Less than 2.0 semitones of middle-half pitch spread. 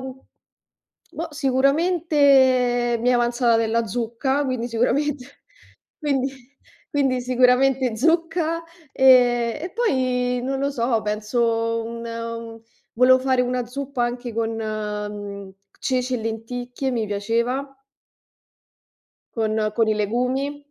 No: average, 2.7 semitones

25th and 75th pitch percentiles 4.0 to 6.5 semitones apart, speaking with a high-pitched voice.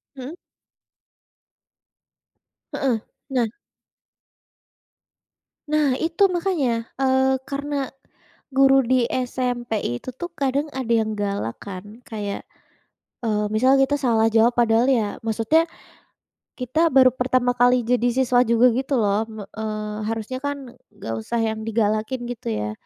No: average, 3.5 semitones; high, 245 Hz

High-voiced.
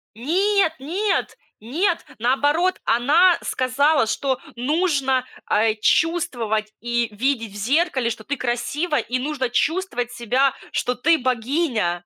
Yes: very high, 260 Hz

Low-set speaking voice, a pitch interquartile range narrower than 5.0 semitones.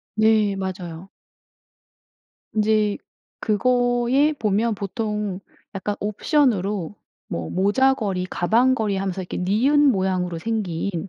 No: high, 205 Hz; average, 3.3 semitones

